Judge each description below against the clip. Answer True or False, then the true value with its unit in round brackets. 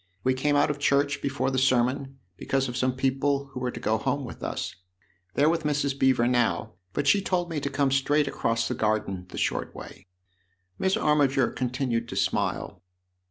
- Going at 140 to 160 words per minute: False (190 wpm)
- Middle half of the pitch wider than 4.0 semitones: False (2.4 semitones)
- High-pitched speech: False (135 Hz)